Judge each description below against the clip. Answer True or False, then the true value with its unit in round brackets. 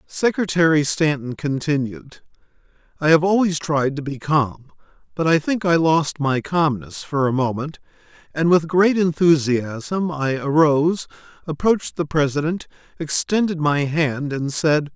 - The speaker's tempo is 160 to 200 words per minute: False (135 wpm)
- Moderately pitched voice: True (155 Hz)